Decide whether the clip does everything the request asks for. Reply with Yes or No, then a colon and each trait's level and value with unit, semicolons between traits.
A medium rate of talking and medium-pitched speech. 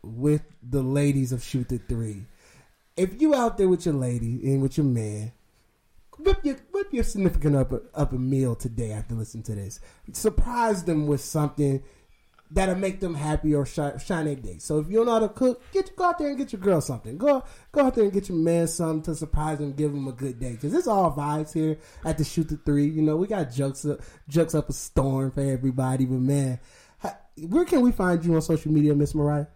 No: fast, 225 wpm; medium, 150 Hz